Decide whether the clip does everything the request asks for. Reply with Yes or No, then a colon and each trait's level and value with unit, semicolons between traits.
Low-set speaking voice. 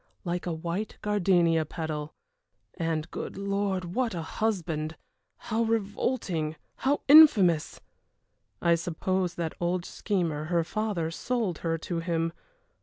No: medium, 175 Hz